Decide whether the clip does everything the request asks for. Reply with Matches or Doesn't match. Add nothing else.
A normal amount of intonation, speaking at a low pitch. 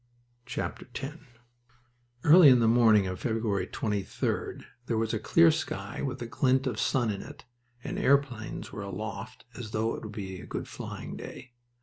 Matches